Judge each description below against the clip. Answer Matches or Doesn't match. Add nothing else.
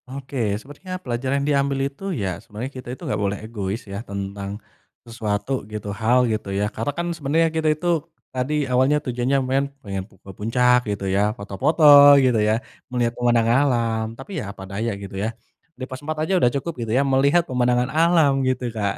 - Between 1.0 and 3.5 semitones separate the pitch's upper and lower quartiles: Doesn't match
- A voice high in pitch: Doesn't match